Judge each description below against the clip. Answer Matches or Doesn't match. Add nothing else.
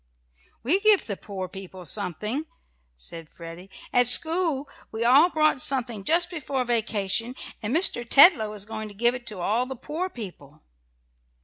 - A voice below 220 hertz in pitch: Doesn't match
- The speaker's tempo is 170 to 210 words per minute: Doesn't match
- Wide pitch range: Matches